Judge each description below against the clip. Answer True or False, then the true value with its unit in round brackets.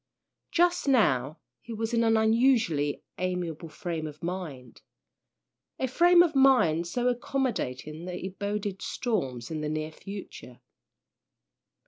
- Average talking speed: False (125 wpm)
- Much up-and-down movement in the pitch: True (7.7 semitones)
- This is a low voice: False (185 Hz)